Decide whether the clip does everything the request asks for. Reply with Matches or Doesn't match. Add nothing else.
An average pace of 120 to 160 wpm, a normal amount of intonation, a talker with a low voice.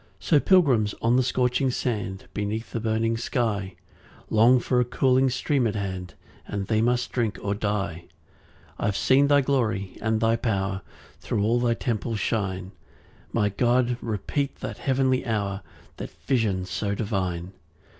Matches